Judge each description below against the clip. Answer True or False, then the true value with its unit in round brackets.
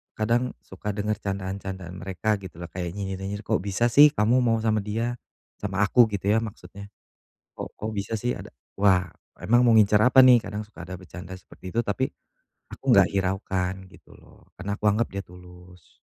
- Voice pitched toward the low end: True (100 Hz)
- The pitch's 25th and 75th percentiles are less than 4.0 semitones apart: True (2.8 semitones)